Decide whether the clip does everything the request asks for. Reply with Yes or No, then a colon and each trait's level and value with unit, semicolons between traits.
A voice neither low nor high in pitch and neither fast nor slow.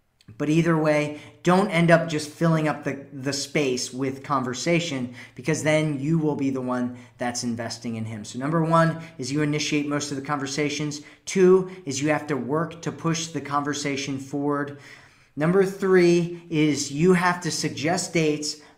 Yes: medium, 150 Hz; average, 175 wpm